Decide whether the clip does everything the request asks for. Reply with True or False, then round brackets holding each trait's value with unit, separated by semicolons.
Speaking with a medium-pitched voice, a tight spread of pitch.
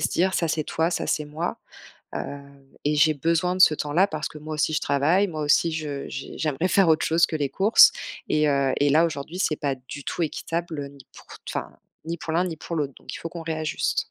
True (155 Hz; 2.3 semitones)